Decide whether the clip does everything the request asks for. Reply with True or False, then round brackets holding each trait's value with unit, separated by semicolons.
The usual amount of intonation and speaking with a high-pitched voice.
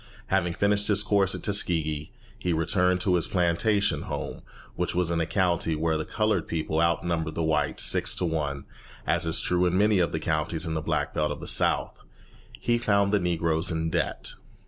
False (3.3 semitones; 85 Hz)